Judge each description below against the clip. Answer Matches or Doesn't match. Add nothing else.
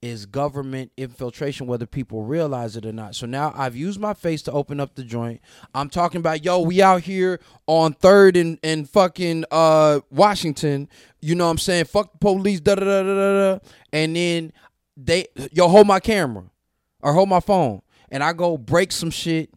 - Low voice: Doesn't match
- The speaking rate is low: Doesn't match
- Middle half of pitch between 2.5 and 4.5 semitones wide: Doesn't match